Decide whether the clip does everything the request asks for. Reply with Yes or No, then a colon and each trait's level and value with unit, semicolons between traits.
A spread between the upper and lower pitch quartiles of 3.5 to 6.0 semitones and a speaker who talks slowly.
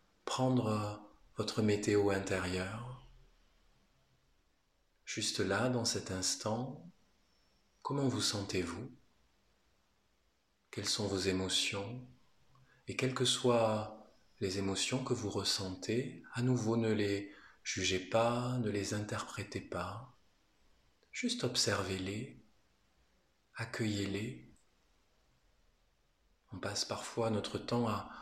Yes: average, 4.1 semitones; slow, 95 wpm